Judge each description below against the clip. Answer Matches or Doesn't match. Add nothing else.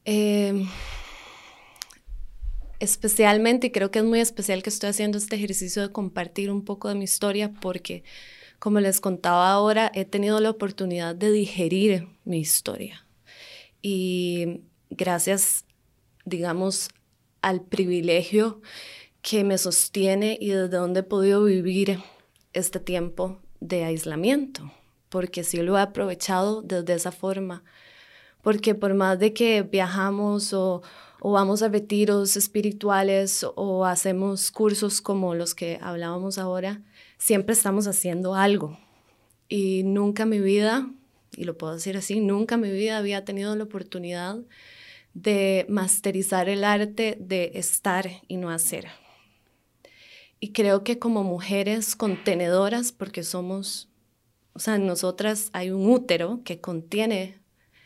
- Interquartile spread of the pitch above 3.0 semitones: Doesn't match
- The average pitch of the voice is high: Matches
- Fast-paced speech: Doesn't match